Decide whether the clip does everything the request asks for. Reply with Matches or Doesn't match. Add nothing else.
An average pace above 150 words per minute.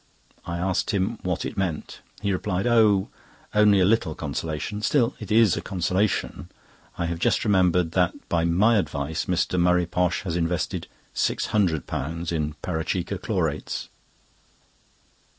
Doesn't match